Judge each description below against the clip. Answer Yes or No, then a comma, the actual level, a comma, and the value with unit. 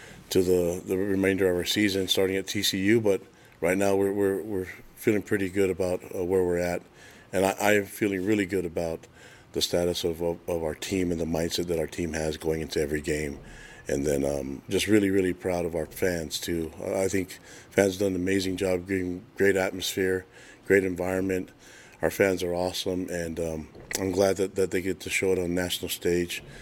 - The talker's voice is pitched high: No, very low, 95 Hz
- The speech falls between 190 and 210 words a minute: Yes, fast, 205 wpm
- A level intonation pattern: Yes, narrow, 1.8 semitones